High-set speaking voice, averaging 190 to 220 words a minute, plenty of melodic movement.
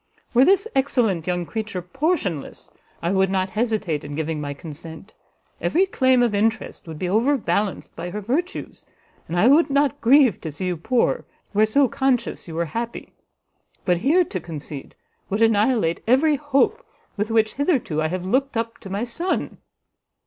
No: high, 220 Hz; average, 170 wpm; wide, 7.1 semitones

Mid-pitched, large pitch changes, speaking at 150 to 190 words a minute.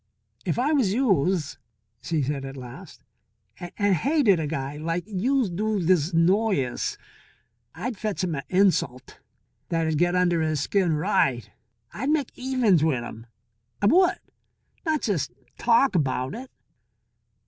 No: medium, 180 Hz; wide, 6.6 semitones; slow, 135 wpm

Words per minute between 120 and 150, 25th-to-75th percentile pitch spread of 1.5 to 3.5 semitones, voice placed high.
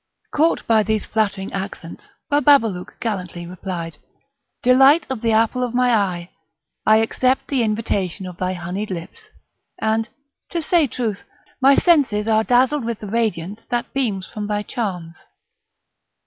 No: average, 145 wpm; average, 4.6 semitones; high, 220 Hz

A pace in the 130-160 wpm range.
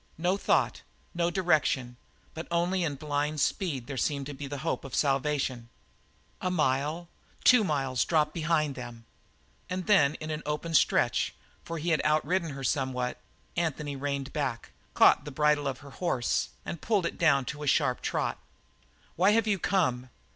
No: average, 170 wpm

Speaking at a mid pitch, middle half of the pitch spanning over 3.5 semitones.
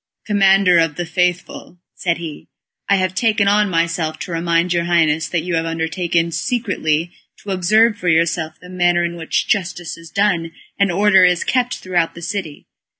No: medium, 175 Hz; narrow, 2.6 semitones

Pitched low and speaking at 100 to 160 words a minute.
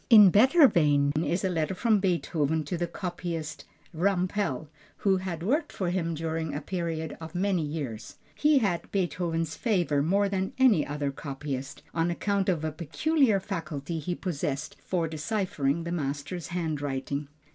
No: medium, 170 Hz; average, 155 wpm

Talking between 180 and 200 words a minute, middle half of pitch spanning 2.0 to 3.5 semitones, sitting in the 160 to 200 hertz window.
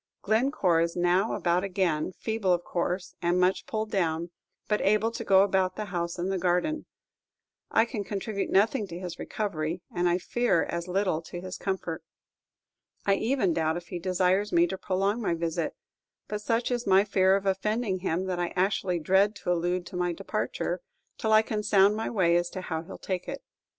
Yes: average, 195 wpm; average, 3.0 semitones; medium, 185 Hz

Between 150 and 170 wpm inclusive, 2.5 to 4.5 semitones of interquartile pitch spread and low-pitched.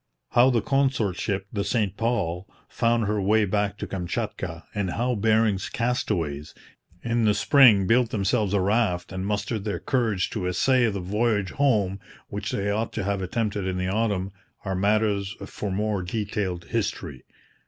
Yes: average, 165 wpm; average, 3.1 semitones; low, 105 Hz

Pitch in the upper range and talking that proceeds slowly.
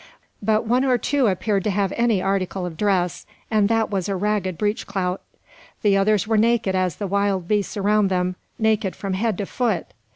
No: high, 200 Hz; average, 195 wpm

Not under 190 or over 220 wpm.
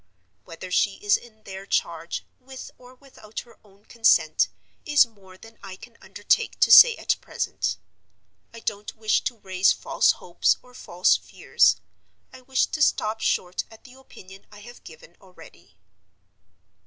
No: average, 155 wpm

